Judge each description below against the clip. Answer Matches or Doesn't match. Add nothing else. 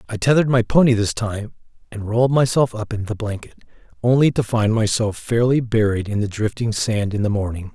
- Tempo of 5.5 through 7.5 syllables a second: Matches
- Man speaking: Matches